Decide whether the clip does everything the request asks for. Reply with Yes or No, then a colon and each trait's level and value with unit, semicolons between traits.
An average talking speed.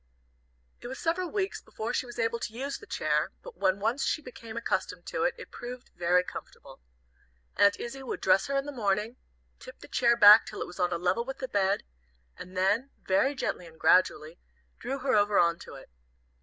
No: fast, 210 wpm